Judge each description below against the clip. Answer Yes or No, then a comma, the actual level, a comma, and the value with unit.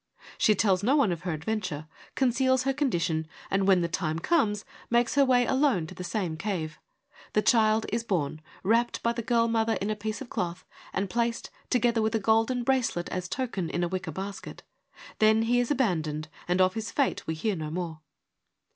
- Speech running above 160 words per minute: Yes, average, 200 wpm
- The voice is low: No, high, 215 Hz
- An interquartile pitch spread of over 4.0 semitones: Yes, average, 5.1 semitones